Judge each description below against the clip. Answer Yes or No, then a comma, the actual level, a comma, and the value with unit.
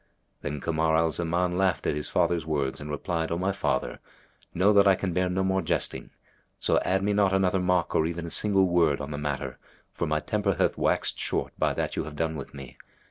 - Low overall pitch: Yes, very low, 85 Hz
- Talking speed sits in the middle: No, fast, 225 wpm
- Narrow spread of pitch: No, average, 3.6 semitones